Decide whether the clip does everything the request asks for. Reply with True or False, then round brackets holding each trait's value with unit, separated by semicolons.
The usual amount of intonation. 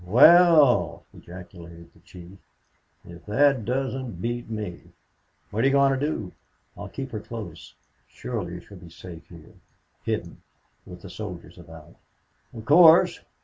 False (7.1 semitones)